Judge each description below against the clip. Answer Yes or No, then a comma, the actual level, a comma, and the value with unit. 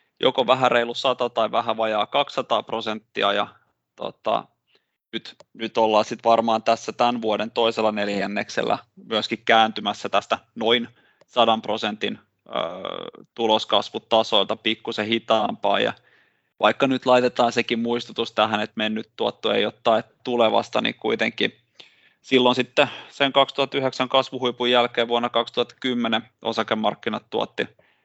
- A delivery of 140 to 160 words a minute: No, average, 120 wpm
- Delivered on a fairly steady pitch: Yes, narrow, 1.9 semitones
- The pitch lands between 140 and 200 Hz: No, low, 115 Hz